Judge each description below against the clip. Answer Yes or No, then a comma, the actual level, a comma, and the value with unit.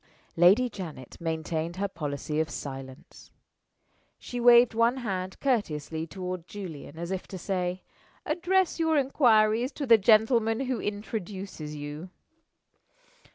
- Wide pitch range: Yes, wide, 6.4 semitones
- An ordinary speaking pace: No, slow, 120 wpm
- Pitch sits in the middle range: No, high, 195 Hz